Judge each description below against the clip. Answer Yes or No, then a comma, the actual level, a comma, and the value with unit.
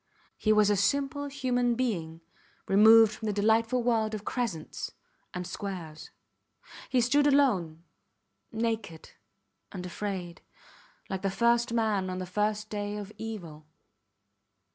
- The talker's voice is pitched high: Yes, high, 215 Hz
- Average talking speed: No, slow, 125 wpm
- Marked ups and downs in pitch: No, average, 3.9 semitones